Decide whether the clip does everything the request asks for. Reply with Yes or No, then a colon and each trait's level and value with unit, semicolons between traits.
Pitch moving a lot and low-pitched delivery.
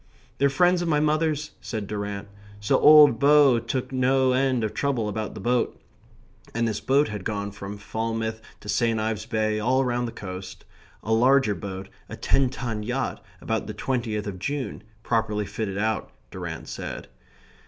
No: average, 4.1 semitones; low, 115 Hz